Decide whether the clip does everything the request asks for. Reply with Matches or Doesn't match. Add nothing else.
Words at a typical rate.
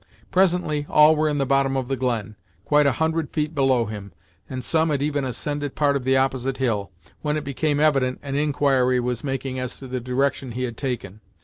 Doesn't match